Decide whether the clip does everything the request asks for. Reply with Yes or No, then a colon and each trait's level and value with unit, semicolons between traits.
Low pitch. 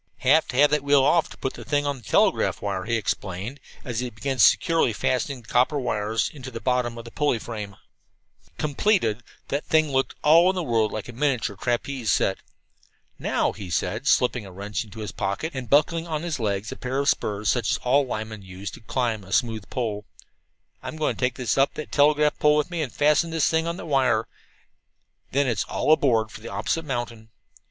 Yes: low, 125 Hz